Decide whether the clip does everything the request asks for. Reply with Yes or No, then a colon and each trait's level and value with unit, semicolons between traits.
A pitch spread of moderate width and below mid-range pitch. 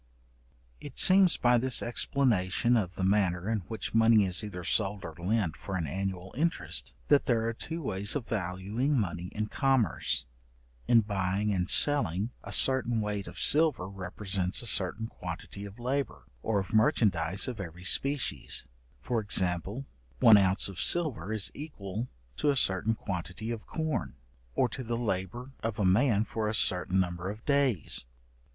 Yes: average, 4.4 semitones; low, 105 Hz